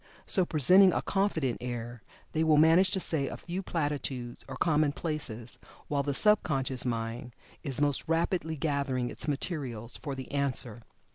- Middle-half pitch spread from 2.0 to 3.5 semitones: No, average, 4.2 semitones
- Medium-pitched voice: Yes, medium, 145 Hz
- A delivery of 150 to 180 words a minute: Yes, average, 155 wpm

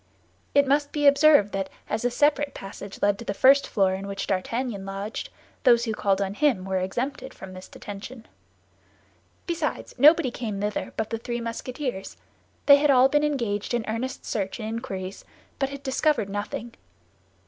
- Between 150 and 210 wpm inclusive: Yes, average, 170 wpm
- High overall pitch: Yes, high, 230 Hz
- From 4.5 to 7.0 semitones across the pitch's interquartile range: Yes, wide, 5.6 semitones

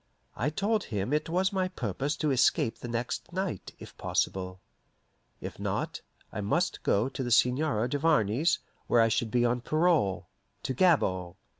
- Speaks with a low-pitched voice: Yes, low, 130 Hz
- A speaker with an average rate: Yes, average, 160 wpm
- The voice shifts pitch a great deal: Yes, wide, 6.6 semitones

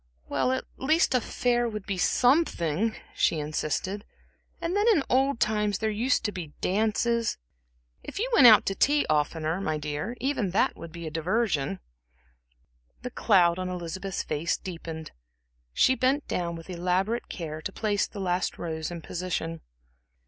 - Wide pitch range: Yes, wide, 6.1 semitones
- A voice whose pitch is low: No, high, 190 Hz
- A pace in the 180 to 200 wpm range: No, average, 160 wpm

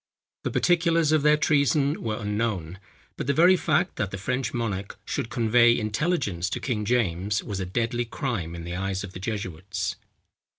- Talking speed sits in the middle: Yes, average, 175 wpm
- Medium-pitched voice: No, low, 115 Hz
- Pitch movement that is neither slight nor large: No, wide, 6.4 semitones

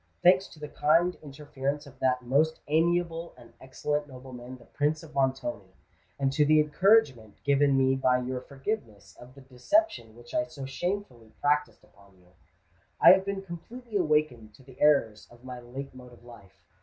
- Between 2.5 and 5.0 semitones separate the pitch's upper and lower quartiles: Yes, average, 4.0 semitones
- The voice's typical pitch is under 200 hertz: Yes, low, 135 Hz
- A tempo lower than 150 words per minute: No, average, 175 wpm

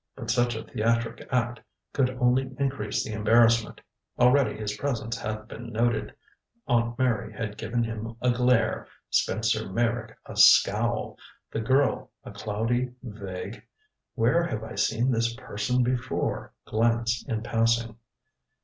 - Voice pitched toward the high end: No, low, 115 Hz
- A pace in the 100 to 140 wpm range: Yes, slow, 135 wpm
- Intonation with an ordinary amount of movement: No, narrow, 2.0 semitones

